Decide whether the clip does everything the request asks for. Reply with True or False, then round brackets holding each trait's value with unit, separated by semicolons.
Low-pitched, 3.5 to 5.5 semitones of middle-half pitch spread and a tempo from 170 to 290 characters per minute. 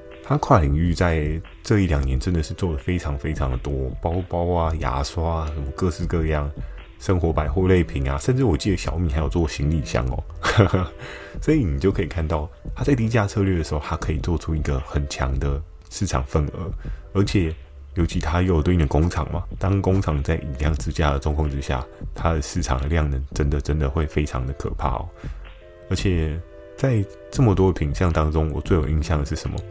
False (80 Hz; 3.9 semitones; 305 characters per minute)